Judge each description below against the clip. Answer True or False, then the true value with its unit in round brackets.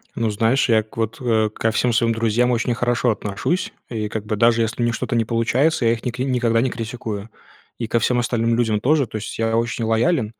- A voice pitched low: True (115 Hz)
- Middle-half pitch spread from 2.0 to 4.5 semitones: False (1.5 semitones)